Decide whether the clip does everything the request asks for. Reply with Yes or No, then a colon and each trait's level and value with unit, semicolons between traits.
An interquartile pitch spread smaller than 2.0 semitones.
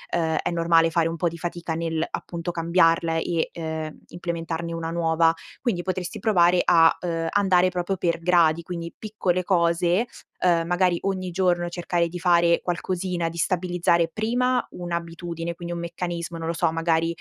Yes: narrow, 1.2 semitones